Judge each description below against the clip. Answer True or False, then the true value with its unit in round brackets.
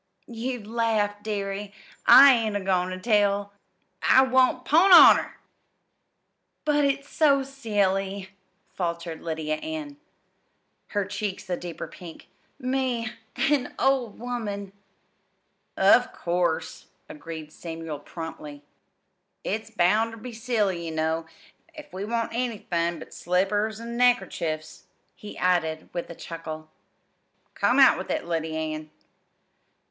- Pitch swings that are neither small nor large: False (5.8 semitones)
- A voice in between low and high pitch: False (205 Hz)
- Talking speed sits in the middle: False (120 wpm)